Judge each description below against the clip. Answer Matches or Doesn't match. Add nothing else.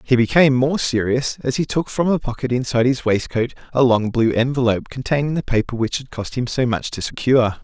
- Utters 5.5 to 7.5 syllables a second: Matches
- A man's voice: Matches